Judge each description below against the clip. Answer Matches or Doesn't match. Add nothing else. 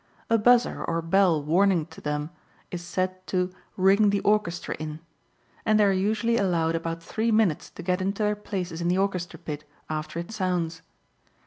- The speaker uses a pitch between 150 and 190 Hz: Matches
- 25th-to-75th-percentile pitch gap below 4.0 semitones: Matches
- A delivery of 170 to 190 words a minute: Matches